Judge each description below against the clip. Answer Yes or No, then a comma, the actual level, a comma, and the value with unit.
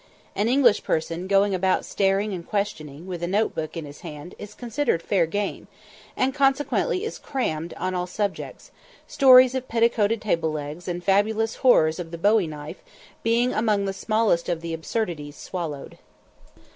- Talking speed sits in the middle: Yes, average, 165 wpm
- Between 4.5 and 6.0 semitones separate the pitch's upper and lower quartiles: Yes, average, 5.1 semitones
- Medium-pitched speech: No, high, 195 Hz